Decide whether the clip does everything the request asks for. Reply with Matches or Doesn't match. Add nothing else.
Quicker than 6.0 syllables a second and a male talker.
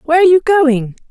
Doesn't match